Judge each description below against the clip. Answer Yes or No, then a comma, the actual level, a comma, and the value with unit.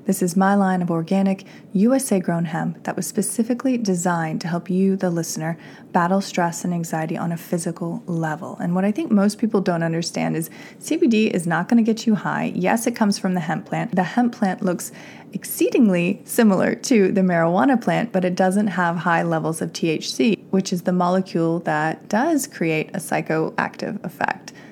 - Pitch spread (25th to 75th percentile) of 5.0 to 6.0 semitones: No, average, 3.7 semitones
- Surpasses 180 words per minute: Yes, average, 190 wpm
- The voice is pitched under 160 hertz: No, medium, 185 Hz